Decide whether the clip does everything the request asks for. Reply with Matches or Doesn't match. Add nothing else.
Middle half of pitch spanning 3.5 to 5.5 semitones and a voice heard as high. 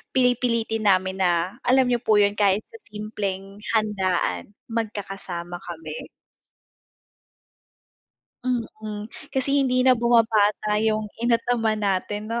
Doesn't match